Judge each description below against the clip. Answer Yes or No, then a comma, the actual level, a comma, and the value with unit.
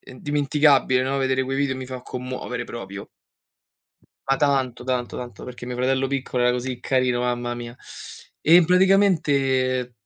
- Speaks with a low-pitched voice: Yes, low, 130 Hz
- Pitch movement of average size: No, narrow, 1.9 semitones